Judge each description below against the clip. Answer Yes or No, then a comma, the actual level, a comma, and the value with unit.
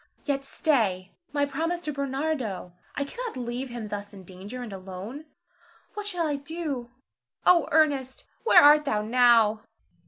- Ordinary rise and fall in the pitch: No, wide, 5.9 semitones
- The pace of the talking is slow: No, average, 150 wpm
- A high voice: Yes, very high, 265 Hz